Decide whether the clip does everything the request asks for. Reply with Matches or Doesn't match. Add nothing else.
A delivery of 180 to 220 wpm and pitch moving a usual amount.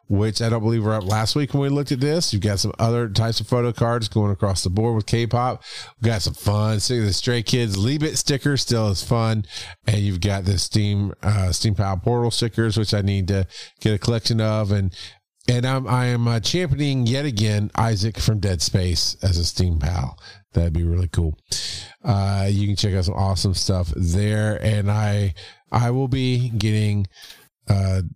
Matches